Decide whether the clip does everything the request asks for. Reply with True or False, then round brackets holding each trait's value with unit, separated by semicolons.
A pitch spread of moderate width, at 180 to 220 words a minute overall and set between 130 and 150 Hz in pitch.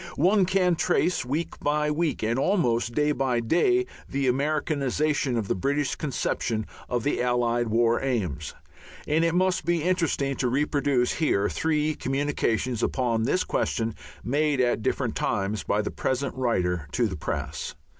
False (4.5 semitones; 150 wpm; 135 Hz)